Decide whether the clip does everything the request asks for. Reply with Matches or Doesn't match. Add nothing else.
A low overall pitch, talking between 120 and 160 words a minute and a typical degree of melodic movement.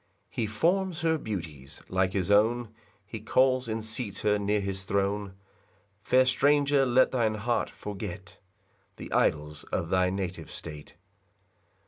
Matches